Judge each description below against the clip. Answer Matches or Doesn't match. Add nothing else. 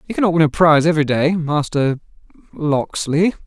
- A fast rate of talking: Doesn't match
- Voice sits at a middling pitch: Matches